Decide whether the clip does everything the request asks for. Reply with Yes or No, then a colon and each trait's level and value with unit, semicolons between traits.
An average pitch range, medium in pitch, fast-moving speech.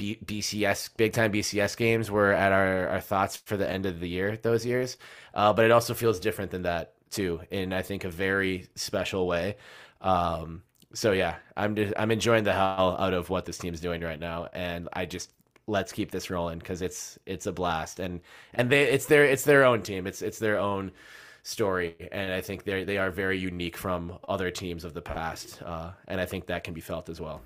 No: average, 3.0 semitones; very low, 95 Hz; fast, 220 wpm